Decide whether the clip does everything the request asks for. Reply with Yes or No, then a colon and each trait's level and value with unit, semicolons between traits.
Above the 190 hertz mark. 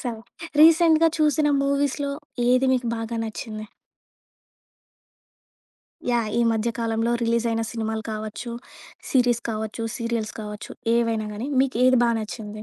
Yes: high, 230 Hz